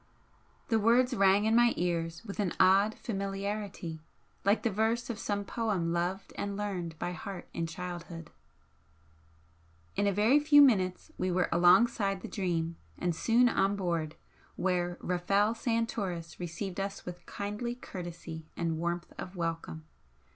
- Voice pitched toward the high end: Yes, high, 195 Hz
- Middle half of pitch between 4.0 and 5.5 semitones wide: No, average, 3.6 semitones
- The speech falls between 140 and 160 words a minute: Yes, average, 145 wpm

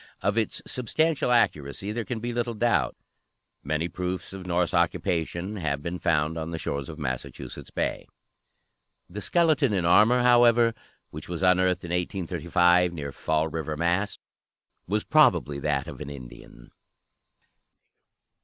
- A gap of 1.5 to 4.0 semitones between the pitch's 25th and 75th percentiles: No, wide, 5.4 semitones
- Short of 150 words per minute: Yes, average, 140 wpm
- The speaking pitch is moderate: No, very low, 90 Hz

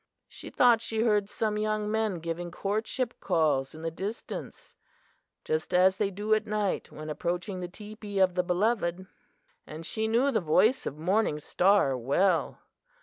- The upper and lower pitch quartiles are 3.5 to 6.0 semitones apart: Yes, average, 4.0 semitones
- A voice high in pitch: Yes, high, 195 Hz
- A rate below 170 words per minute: Yes, average, 160 wpm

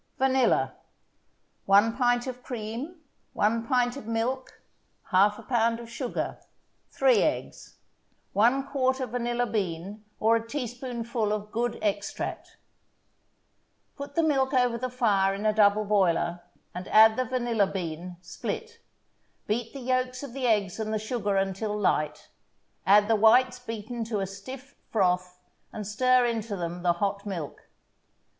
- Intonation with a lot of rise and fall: No, average, 3.7 semitones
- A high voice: Yes, high, 225 Hz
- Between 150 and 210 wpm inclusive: No, average, 140 wpm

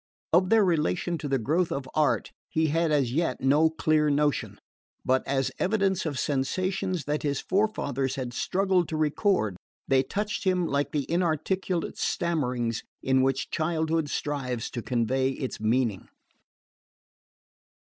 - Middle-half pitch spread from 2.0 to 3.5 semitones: No, average, 4.6 semitones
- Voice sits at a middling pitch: Yes, medium, 150 Hz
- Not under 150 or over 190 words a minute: No, average, 140 wpm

